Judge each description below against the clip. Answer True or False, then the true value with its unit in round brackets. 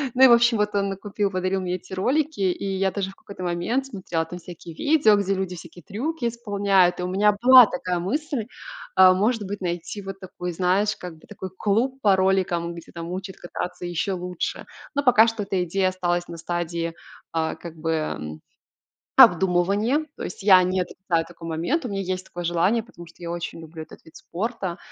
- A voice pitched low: False (185 Hz)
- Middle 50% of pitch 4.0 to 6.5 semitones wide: False (3.1 semitones)